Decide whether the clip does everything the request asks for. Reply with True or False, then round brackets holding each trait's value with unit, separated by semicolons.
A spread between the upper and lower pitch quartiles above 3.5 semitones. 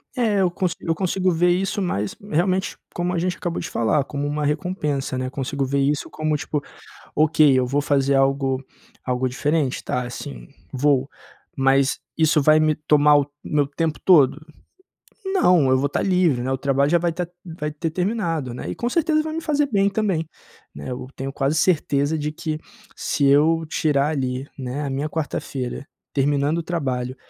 True (4.0 semitones)